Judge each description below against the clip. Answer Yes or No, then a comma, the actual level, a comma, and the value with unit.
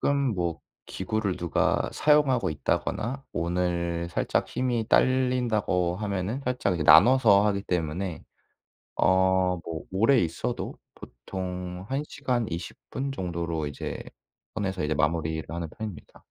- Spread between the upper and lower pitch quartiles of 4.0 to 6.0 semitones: Yes, average, 5.3 semitones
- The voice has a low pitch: Yes, very low, 95 Hz